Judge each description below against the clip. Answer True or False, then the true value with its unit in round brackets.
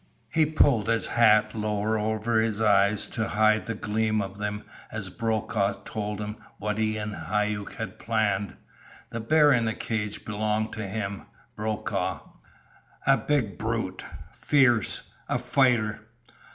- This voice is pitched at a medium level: False (110 Hz)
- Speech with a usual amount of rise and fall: False (1.3 semitones)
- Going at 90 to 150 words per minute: True (140 wpm)